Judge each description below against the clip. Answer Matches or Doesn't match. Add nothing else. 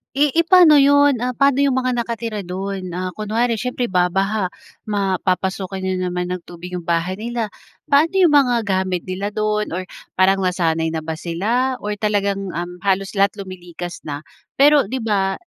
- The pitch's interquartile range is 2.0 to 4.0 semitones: Doesn't match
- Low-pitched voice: Doesn't match